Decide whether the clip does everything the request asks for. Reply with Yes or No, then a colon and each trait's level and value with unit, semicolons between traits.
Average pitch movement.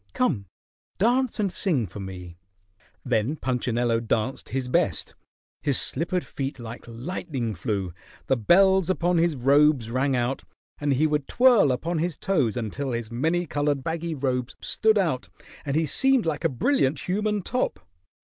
No: wide, 6.3 semitones